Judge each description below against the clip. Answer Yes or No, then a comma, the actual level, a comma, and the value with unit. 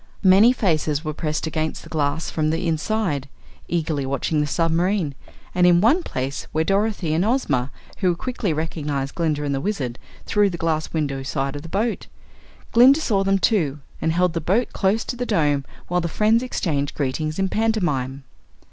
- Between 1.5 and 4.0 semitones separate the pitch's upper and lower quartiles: No, average, 5.1 semitones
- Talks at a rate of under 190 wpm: Yes, average, 175 wpm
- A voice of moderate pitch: Yes, medium, 165 Hz